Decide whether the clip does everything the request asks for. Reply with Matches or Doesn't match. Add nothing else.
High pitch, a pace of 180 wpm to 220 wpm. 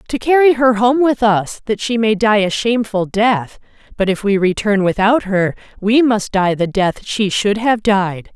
Matches